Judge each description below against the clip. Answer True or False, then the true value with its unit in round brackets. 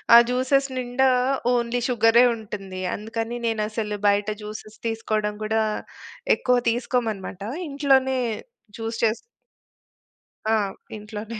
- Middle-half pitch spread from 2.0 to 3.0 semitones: True (2.5 semitones)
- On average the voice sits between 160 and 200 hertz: False (225 Hz)